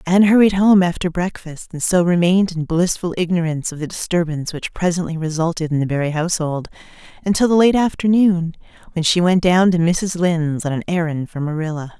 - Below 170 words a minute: No, average, 185 wpm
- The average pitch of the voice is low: No, medium, 170 Hz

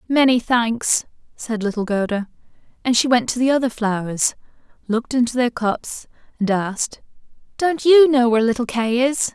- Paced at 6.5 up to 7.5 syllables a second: No, 5.0 syllables/s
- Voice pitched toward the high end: Yes, high, 240 Hz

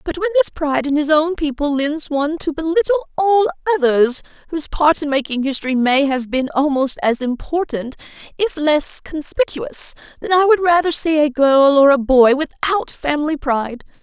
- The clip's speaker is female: Yes, female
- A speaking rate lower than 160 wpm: No, average, 170 wpm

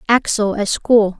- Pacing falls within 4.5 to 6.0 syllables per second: No, 3.9 syllables/s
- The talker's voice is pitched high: Yes, high, 215 Hz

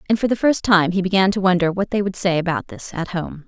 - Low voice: No, medium, 185 Hz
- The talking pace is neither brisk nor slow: No, fast, 295 wpm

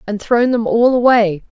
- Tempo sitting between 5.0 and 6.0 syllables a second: No, 4.5 syllables/s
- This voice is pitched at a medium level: No, high, 225 Hz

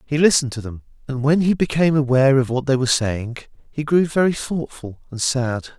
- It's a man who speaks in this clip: Yes, male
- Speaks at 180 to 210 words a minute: Yes, fast, 205 wpm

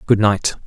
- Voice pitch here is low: Yes, low, 105 Hz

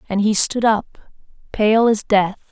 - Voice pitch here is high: Yes, high, 210 Hz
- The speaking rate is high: No, average, 165 wpm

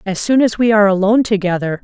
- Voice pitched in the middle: No, high, 205 Hz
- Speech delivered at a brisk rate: Yes, fast, 230 wpm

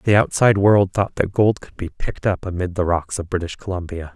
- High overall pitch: No, very low, 95 Hz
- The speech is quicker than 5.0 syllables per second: Yes, 5.6 syllables/s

